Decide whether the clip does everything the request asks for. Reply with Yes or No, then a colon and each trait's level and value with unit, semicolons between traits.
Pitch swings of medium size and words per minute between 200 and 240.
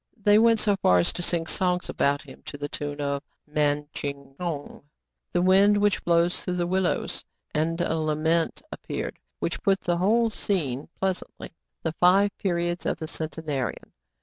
No: average, 4.2 semitones; average, 175 wpm